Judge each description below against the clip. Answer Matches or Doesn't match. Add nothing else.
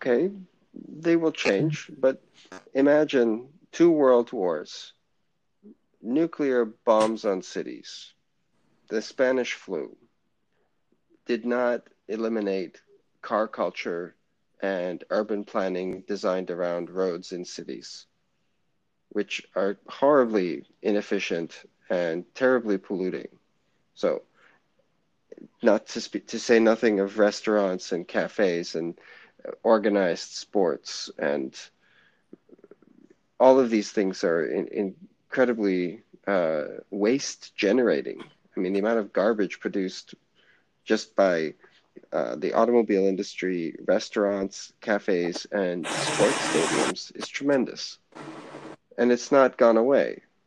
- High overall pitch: Doesn't match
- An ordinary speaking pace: Doesn't match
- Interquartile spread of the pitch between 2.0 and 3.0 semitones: Doesn't match